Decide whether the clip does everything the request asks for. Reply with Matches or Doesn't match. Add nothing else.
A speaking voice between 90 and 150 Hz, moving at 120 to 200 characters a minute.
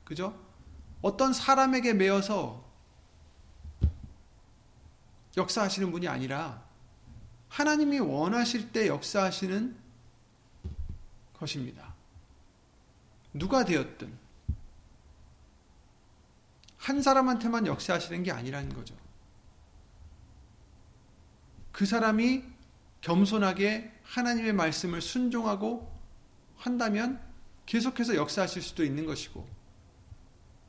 Doesn't match